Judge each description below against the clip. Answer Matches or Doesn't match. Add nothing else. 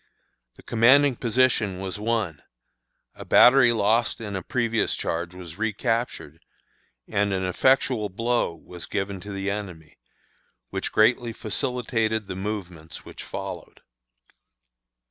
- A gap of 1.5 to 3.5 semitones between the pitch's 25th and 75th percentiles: Doesn't match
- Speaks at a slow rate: Matches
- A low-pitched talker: Matches